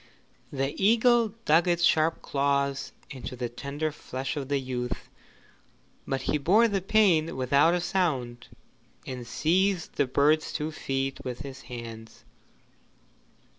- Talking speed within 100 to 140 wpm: Yes, slow, 135 wpm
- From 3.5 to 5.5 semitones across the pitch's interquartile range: Yes, average, 4.6 semitones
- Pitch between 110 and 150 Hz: Yes, medium, 140 Hz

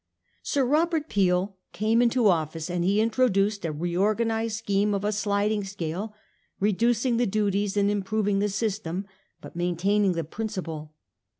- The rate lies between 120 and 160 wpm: Yes, average, 140 wpm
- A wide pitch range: No, average, 3.0 semitones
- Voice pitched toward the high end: Yes, high, 205 Hz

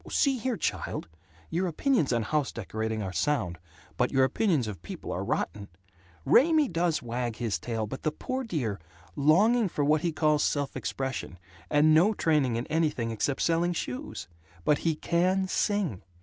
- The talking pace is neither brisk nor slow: Yes, average, 165 wpm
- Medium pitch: Yes, medium, 150 Hz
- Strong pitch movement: Yes, wide, 6.9 semitones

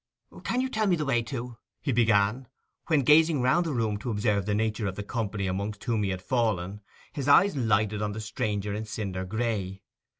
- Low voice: Yes, low, 110 Hz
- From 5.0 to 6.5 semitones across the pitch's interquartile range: No, average, 4.0 semitones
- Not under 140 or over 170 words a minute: No, fast, 205 wpm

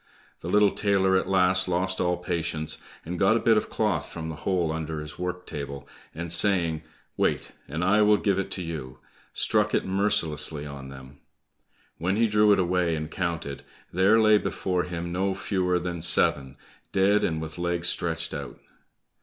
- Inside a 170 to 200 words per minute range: Yes, average, 180 wpm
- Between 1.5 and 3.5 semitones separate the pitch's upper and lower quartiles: Yes, average, 3.1 semitones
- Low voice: Yes, very low, 90 Hz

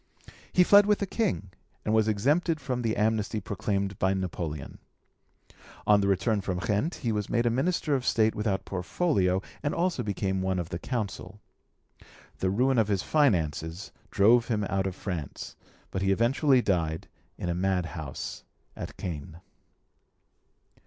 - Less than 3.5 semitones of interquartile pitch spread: No, average, 4.7 semitones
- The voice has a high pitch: No, low, 100 Hz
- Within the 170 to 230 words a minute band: No, average, 155 wpm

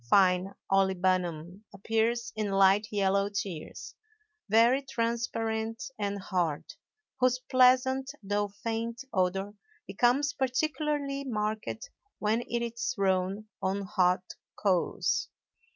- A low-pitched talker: No, high, 210 Hz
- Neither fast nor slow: No, slow, 100 wpm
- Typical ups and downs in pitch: Yes, average, 3.6 semitones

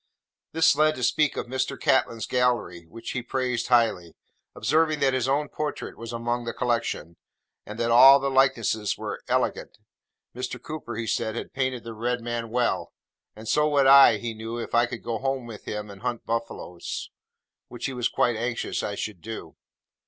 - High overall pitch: No, low, 120 Hz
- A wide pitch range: No, average, 2.7 semitones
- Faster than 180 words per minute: Yes, average, 190 wpm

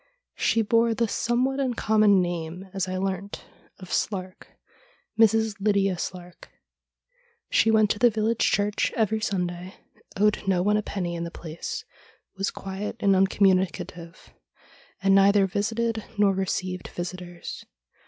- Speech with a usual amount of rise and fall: Yes, average, 3.0 semitones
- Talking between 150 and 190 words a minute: No, average, 140 wpm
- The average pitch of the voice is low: No, high, 195 Hz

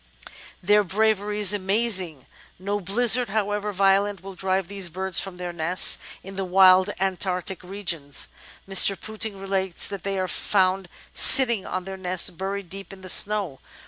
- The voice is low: No, high, 195 Hz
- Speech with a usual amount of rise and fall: No, narrow, 1.8 semitones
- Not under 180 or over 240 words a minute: No, average, 160 wpm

